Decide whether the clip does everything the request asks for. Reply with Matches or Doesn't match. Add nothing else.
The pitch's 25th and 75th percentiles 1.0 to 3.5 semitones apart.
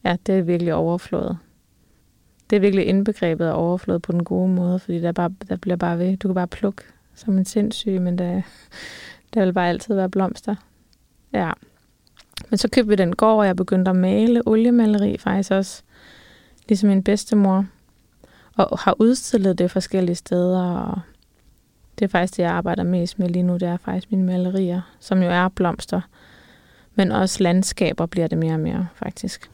Matches